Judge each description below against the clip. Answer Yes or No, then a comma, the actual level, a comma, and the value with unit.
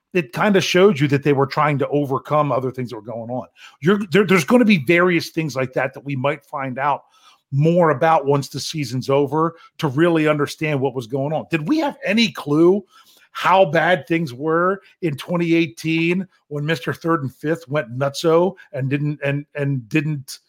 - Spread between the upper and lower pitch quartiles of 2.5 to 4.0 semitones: Yes, average, 3.5 semitones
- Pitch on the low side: No, medium, 155 Hz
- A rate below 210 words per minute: Yes, average, 200 wpm